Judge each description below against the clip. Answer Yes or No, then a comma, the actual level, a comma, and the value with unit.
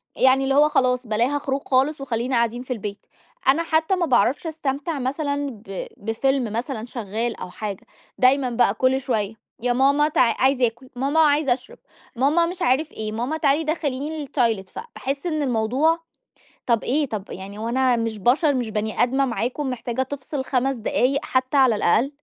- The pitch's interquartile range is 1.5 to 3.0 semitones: No, average, 3.5 semitones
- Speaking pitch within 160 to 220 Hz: No, very high, 260 Hz